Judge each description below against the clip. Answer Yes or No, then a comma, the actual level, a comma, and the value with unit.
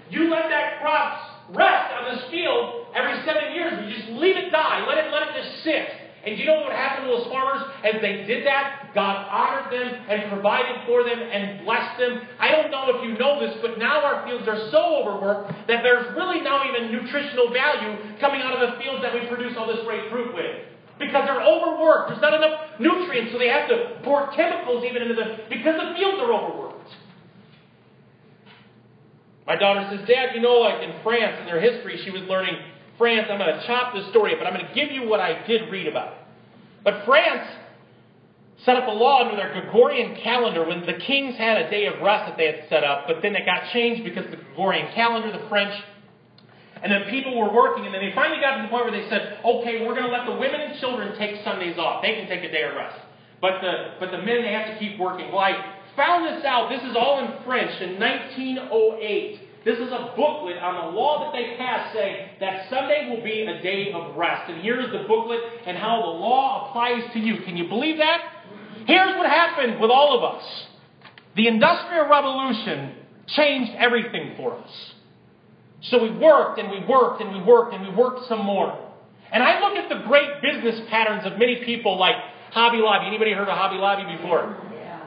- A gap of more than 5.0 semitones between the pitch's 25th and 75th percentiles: Yes, wide, 5.4 semitones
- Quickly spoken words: Yes, fast, 215 wpm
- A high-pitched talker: Yes, high, 235 Hz